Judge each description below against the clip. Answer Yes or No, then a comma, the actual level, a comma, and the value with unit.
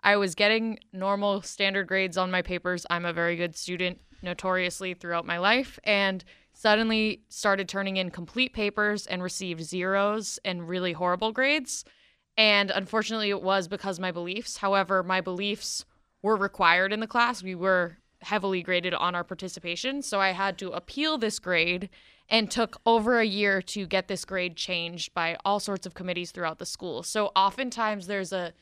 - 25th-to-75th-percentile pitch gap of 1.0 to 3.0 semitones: Yes, narrow, 2.5 semitones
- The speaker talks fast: No, average, 175 wpm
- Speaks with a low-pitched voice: No, high, 195 Hz